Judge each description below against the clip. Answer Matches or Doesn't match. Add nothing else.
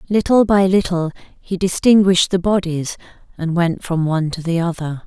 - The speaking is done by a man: Doesn't match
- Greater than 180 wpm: Doesn't match